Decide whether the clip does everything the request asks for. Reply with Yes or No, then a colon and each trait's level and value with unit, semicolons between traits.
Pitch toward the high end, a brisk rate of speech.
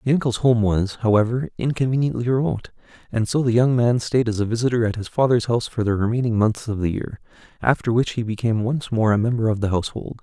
No: low, 115 Hz; fast, 225 wpm